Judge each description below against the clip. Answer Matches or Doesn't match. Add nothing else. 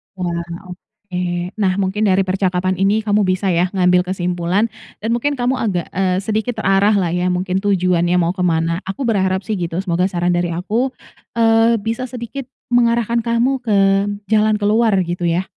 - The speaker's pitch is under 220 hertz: Matches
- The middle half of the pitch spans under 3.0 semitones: Doesn't match